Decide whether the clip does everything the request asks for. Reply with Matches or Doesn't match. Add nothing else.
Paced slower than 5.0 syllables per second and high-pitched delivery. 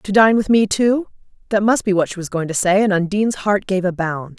Doesn't match